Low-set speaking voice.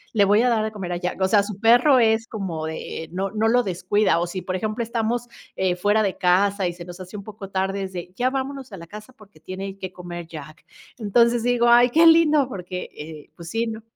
No: high, 200 Hz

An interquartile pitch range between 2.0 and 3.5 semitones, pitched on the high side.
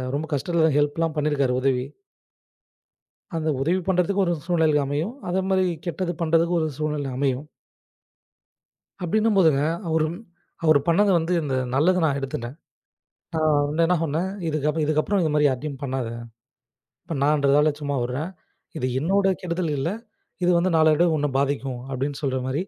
No: average, 3.2 semitones; medium, 155 Hz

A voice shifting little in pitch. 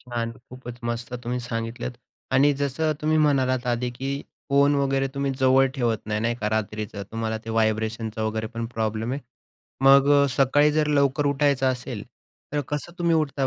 No: average, 3.6 semitones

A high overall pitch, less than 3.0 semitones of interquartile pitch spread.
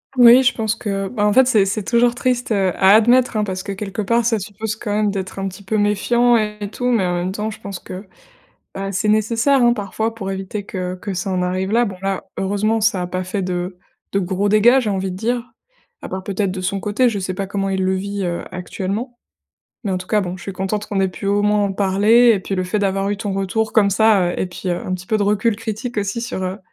Yes: high, 200 Hz; narrow, 2.6 semitones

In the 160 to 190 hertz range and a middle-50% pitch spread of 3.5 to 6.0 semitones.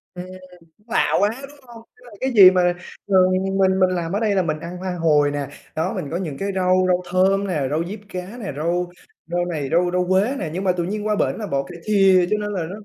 No: medium, 185 Hz; narrow, 2.6 semitones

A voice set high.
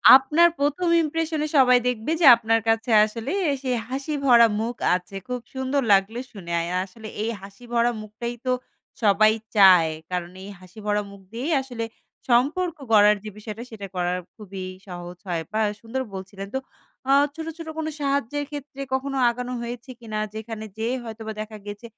Yes: high, 230 Hz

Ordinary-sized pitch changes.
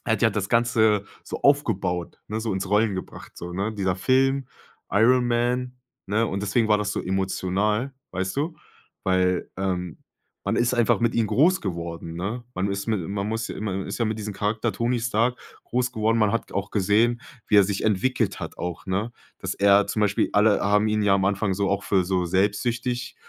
Yes: average, 3.3 semitones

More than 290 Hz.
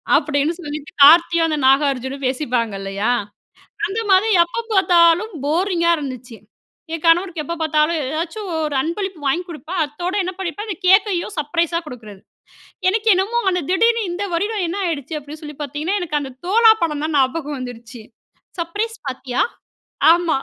Yes: very high, 330 Hz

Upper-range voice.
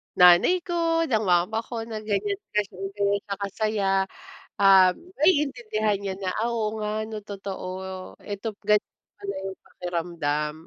Yes: high, 205 Hz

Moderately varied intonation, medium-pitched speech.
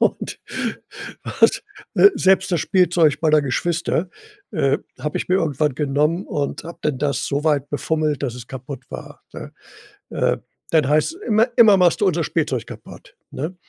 Yes: average, 3.5 semitones; medium, 155 Hz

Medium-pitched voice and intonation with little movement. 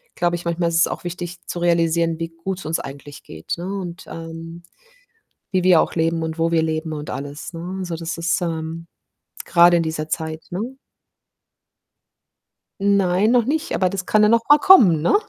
Yes: medium, 170 Hz; narrow, 2.0 semitones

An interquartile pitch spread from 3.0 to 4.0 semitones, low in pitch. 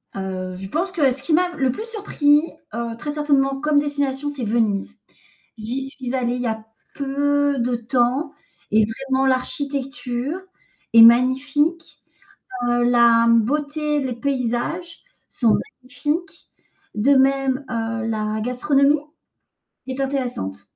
No: average, 3.5 semitones; very high, 265 Hz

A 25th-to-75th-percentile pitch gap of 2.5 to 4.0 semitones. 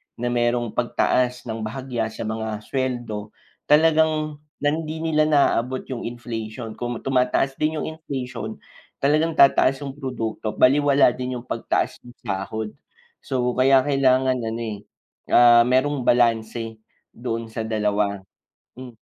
Yes: average, 3.4 semitones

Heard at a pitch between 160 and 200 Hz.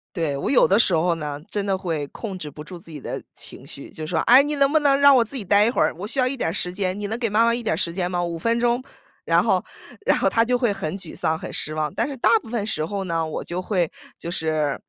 Yes: high, 190 Hz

